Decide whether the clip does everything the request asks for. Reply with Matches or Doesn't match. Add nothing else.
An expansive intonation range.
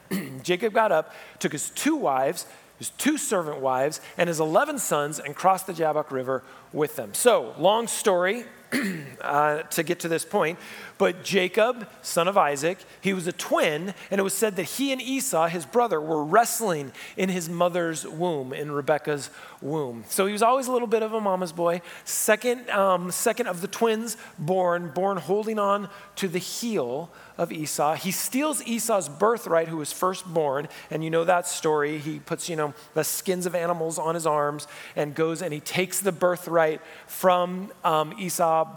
Doesn't match